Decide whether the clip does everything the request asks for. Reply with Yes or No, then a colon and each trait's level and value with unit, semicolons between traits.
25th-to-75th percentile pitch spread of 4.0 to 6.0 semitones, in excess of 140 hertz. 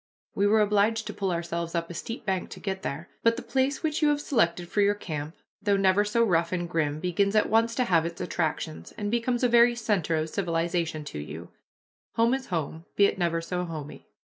Yes: average, 5.0 semitones; high, 190 Hz